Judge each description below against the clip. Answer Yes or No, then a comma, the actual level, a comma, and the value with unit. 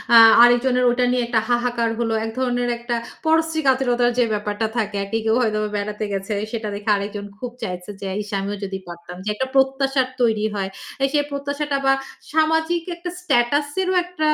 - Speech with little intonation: No, average, 4.5 semitones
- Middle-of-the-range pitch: No, high, 240 Hz